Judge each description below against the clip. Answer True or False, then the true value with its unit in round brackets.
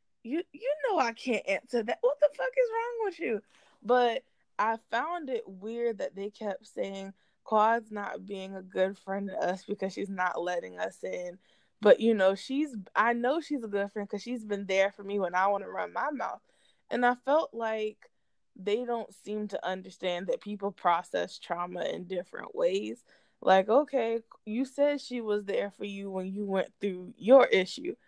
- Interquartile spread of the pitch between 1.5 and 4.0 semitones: False (4.5 semitones)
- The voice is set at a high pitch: True (215 Hz)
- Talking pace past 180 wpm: True (195 wpm)